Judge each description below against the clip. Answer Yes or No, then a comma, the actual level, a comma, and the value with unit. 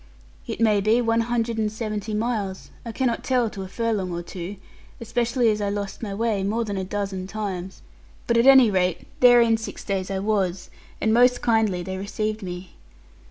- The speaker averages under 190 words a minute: No, average, 195 wpm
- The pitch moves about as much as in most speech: Yes, average, 3.1 semitones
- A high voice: Yes, high, 215 Hz